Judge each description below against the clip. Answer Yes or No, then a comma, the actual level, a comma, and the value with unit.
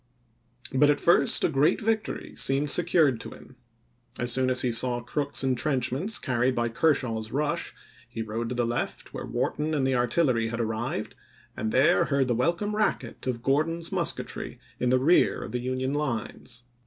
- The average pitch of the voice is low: Yes, low, 130 Hz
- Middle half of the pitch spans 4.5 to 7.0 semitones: No, average, 3.8 semitones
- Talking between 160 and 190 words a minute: Yes, average, 180 wpm